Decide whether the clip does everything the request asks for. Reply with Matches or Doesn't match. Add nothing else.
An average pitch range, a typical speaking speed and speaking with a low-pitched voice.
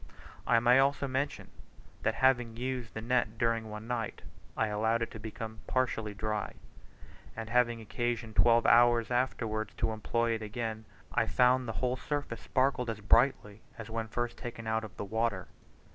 Doesn't match